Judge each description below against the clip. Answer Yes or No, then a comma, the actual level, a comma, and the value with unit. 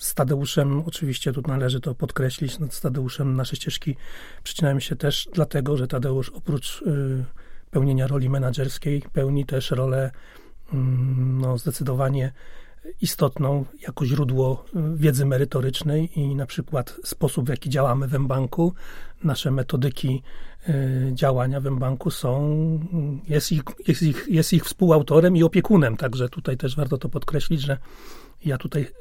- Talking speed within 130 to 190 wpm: Yes, average, 140 wpm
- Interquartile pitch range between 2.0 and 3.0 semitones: Yes, narrow, 2.5 semitones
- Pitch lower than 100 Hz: No, medium, 140 Hz